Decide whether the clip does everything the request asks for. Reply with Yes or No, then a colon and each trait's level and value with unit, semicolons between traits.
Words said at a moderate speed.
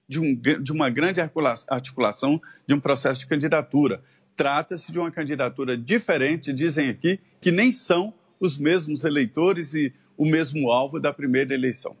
Yes: average, 155 wpm